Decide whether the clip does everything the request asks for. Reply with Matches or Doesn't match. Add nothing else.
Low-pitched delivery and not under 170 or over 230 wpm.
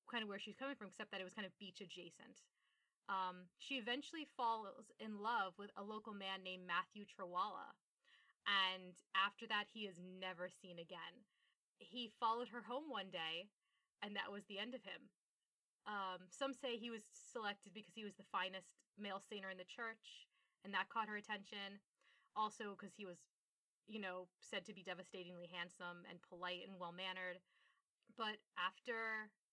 Doesn't match